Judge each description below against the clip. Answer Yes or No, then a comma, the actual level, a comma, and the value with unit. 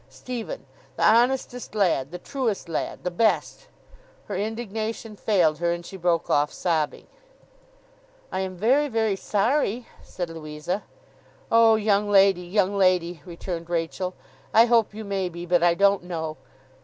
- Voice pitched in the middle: No, high, 195 Hz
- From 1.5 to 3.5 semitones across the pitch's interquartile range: No, average, 4.3 semitones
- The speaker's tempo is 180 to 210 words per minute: No, average, 145 wpm